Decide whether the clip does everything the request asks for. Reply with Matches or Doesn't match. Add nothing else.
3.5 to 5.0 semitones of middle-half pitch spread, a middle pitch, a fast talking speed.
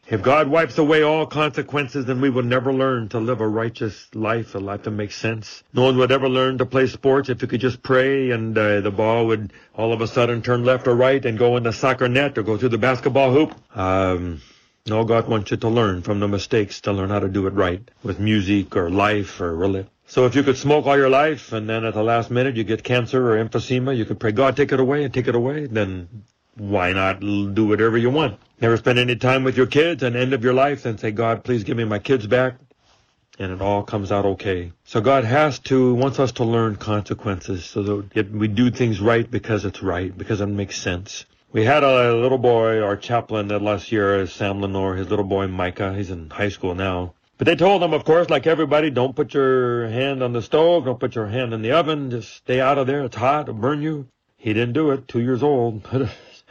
Doesn't match